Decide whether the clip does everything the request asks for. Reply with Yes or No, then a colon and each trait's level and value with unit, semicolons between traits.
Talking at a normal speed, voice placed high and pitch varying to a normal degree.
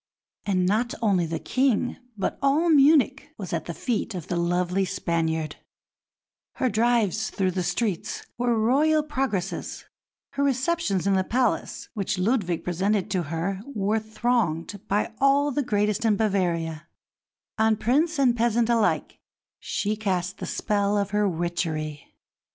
Yes: average, 145 wpm; high, 210 Hz; average, 5.0 semitones